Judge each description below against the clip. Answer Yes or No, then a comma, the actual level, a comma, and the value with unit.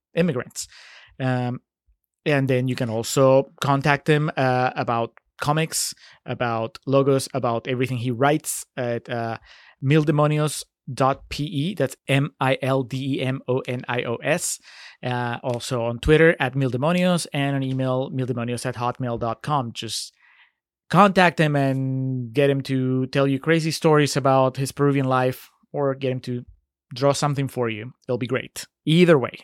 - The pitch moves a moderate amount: No, narrow, 2.3 semitones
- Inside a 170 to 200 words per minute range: No, average, 150 wpm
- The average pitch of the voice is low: Yes, low, 130 Hz